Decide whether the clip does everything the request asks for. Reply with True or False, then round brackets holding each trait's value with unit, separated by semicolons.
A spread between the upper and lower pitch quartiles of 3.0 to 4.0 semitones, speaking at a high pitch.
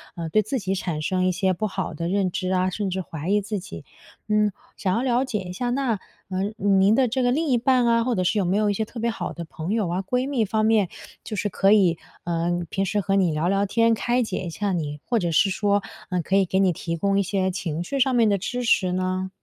True (3.4 semitones; 195 Hz)